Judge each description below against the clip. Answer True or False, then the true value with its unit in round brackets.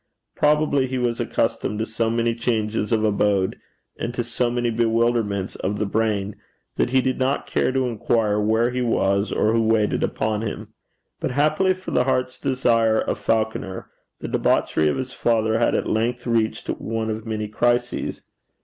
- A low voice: True (115 Hz)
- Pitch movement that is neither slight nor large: False (2.2 semitones)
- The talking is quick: False (175 wpm)